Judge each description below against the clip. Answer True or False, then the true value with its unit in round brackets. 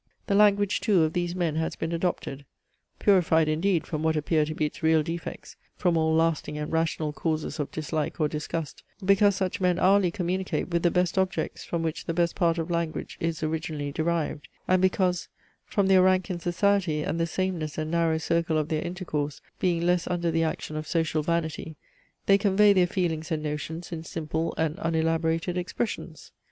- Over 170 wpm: True (190 wpm)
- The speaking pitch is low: False (165 Hz)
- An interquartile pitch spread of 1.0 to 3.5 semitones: True (2.4 semitones)